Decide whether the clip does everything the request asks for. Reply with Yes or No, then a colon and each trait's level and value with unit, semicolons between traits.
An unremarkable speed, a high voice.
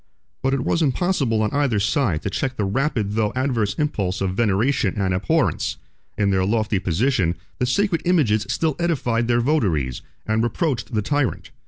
No: average, 170 wpm; low, 115 Hz